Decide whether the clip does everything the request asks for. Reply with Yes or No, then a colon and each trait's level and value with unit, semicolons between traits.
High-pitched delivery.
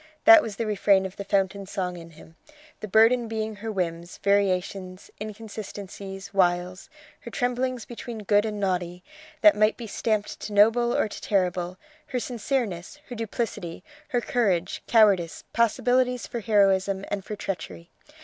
Yes: high, 205 Hz